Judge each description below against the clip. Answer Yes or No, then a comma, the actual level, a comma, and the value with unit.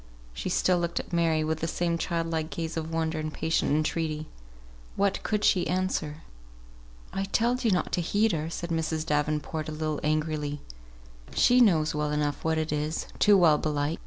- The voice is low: No, medium, 160 Hz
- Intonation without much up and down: Yes, narrow, 2.1 semitones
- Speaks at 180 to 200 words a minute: Yes, average, 185 wpm